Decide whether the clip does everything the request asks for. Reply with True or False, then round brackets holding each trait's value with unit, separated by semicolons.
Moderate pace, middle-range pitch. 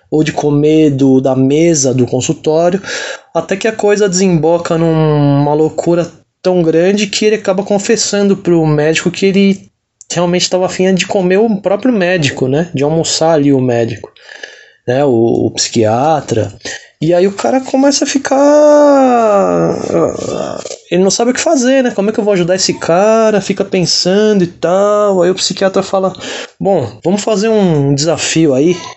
True (165 wpm; 180 Hz)